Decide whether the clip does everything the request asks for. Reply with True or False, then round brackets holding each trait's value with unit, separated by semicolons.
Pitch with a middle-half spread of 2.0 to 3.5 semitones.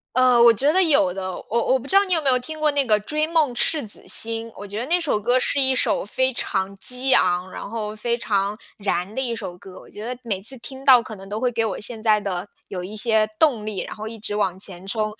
False (4.2 semitones)